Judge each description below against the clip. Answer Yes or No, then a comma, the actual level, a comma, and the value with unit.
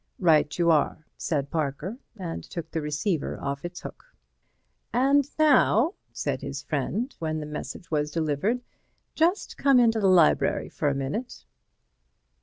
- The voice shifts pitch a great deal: Yes, wide, 8.0 semitones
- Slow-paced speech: No, average, 145 wpm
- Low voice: No, medium, 170 Hz